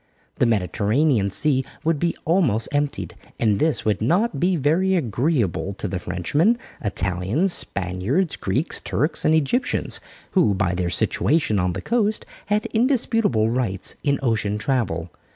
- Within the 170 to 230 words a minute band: No, average, 140 wpm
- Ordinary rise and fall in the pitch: No, wide, 8.8 semitones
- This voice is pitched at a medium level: No, low, 130 Hz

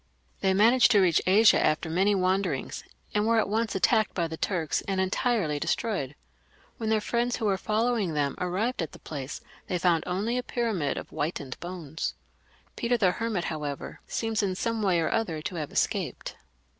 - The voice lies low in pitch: No, high, 190 Hz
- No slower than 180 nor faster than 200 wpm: Yes, average, 185 wpm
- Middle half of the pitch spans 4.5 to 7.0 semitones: Yes, average, 5.1 semitones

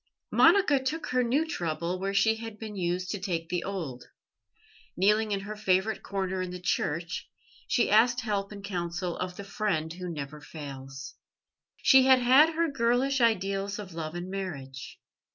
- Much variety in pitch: No, average, 4.6 semitones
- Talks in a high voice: Yes, high, 195 Hz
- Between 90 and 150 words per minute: No, average, 170 wpm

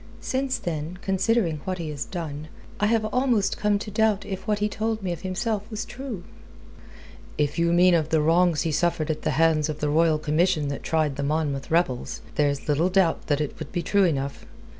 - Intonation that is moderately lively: Yes, average, 4.9 semitones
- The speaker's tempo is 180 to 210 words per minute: Yes, fast, 205 wpm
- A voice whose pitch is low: No, medium, 170 Hz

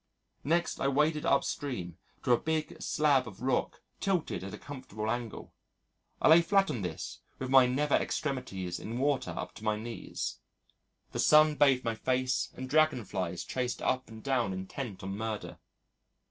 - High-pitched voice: No, low, 130 Hz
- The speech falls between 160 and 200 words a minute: Yes, average, 165 wpm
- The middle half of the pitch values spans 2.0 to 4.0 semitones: No, average, 5.1 semitones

